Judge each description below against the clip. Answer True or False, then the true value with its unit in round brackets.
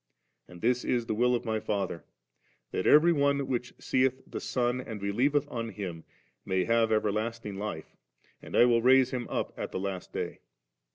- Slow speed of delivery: False (180 wpm)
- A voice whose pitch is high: False (115 Hz)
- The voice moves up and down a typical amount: True (3.7 semitones)